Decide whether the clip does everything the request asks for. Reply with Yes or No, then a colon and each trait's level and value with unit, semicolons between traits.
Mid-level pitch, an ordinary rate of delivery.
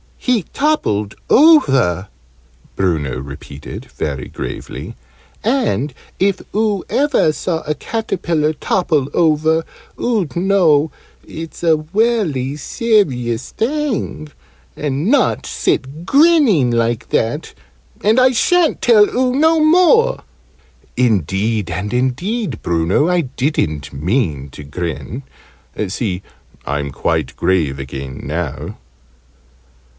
No: medium, 150 Hz; slow, 100 wpm